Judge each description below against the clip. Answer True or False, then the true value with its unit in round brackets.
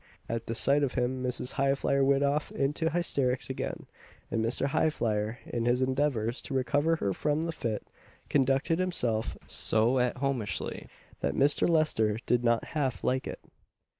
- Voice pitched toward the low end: True (130 Hz)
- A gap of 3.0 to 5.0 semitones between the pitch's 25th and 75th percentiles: True (3.6 semitones)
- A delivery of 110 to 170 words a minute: True (160 wpm)